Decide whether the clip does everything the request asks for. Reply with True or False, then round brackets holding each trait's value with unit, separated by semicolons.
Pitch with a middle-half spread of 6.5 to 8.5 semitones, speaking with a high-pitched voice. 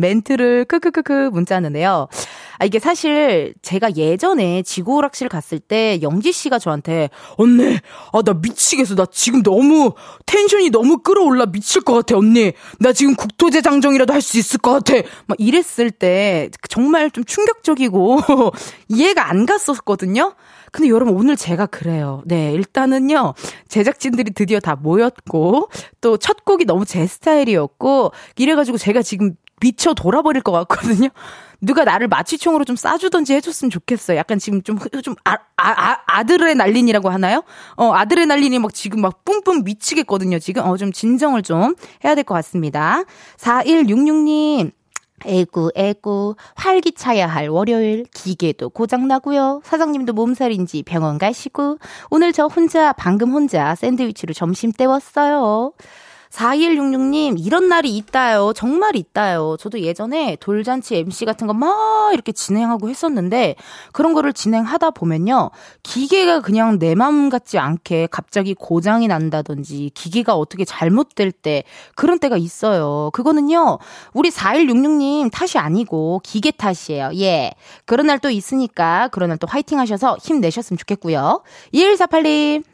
True (7.3 semitones; 240 Hz)